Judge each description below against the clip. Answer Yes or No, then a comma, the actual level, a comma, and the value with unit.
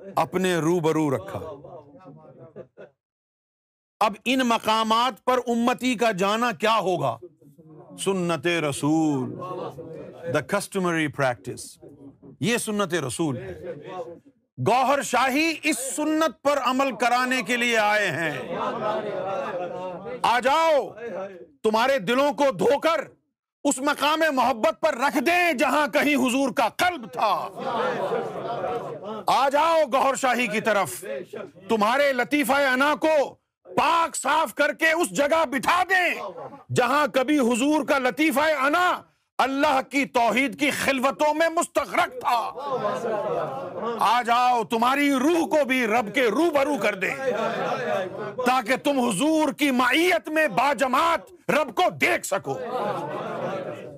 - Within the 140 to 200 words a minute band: No, average, 120 wpm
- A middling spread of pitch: No, wide, 6.2 semitones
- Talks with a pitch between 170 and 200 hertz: No, very high, 255 Hz